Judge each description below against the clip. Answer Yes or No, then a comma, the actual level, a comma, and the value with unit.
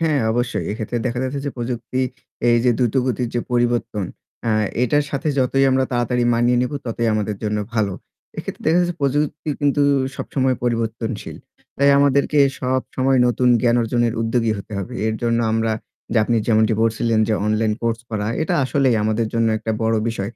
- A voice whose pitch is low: Yes, low, 120 Hz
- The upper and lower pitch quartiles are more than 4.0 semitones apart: No, narrow, 2.5 semitones